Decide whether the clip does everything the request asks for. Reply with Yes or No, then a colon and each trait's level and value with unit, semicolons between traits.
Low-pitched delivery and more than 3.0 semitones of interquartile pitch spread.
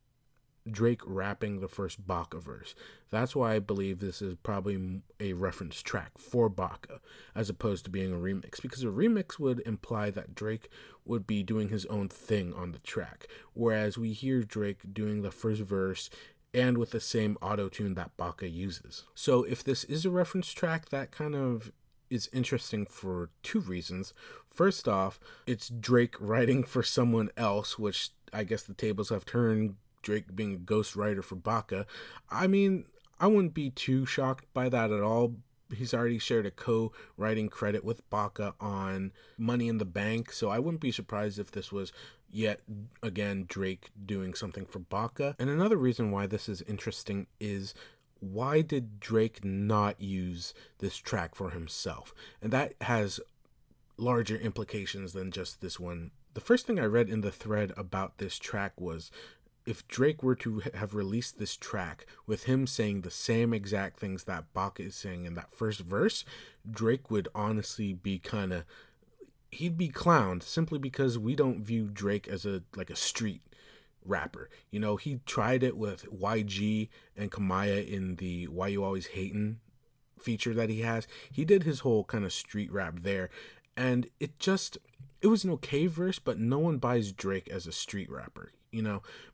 Yes: low, 110 Hz; average, 3.8 semitones